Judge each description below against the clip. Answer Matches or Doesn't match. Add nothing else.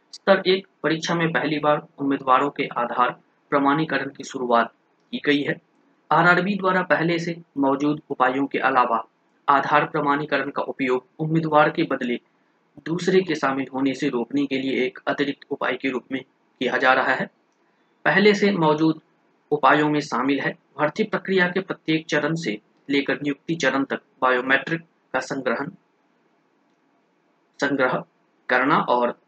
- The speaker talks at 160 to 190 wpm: Doesn't match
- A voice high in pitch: Doesn't match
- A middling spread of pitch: Matches